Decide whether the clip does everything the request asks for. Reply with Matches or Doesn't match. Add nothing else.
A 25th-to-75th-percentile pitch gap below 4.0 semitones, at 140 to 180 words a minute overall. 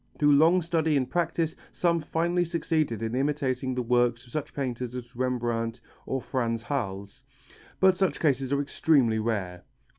Doesn't match